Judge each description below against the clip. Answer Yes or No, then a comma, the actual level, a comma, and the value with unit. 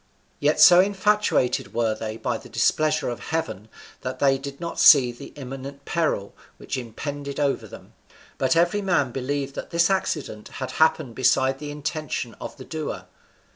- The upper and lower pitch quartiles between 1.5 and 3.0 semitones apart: No, average, 3.7 semitones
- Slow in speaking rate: No, average, 165 wpm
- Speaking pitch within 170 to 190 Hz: No, medium, 140 Hz